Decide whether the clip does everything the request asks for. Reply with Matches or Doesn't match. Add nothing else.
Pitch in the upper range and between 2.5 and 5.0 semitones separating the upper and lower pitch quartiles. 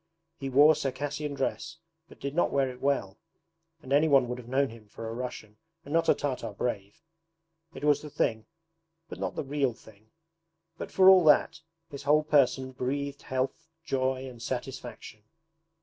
Doesn't match